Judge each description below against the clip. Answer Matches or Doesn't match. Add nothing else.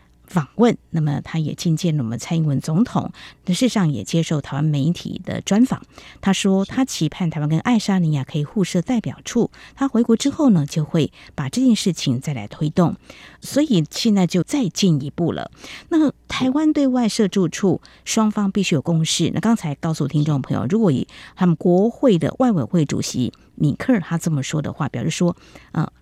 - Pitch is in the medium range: Matches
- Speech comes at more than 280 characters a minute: Matches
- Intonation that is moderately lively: Doesn't match